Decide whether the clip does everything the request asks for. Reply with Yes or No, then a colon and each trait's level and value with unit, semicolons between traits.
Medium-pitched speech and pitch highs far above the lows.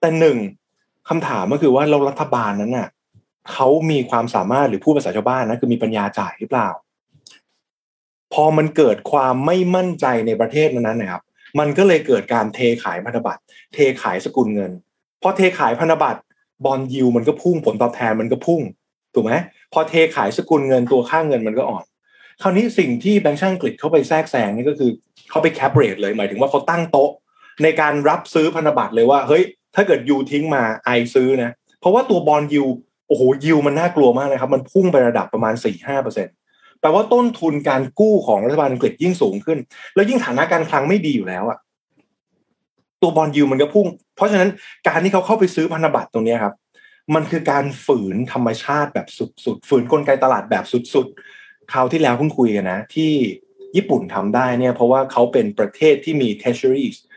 Yes: medium, 150 Hz; wide, 5.7 semitones